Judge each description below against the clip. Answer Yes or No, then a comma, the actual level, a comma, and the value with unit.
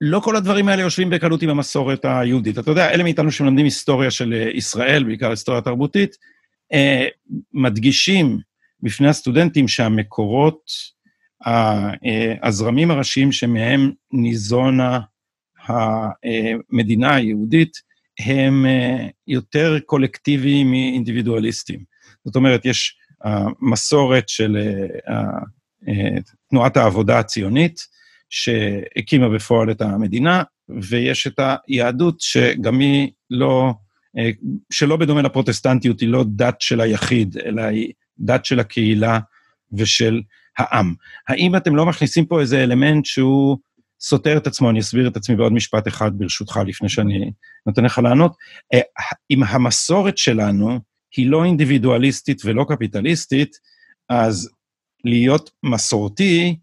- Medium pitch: No, low, 125 Hz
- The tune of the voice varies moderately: Yes, average, 4.4 semitones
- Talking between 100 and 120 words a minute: Yes, average, 110 wpm